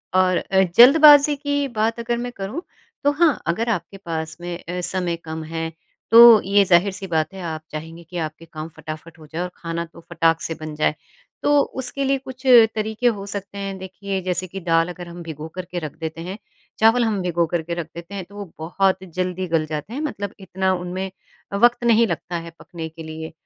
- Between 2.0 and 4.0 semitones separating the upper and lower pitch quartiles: No, average, 4.6 semitones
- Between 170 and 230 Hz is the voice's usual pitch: Yes, medium, 185 Hz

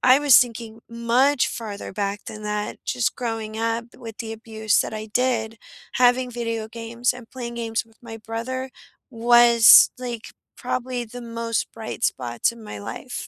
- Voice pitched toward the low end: No, high, 230 Hz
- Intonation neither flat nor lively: No, narrow, 1.6 semitones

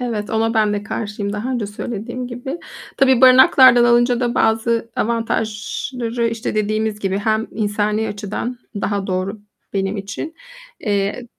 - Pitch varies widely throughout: No, narrow, 2.6 semitones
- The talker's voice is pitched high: Yes, high, 220 Hz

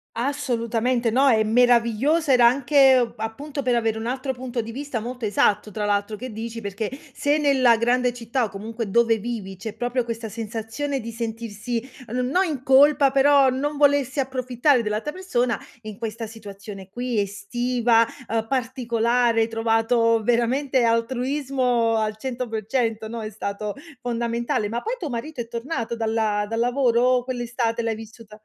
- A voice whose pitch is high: Yes, high, 235 Hz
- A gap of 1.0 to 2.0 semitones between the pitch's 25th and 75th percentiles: No, narrow, 2.5 semitones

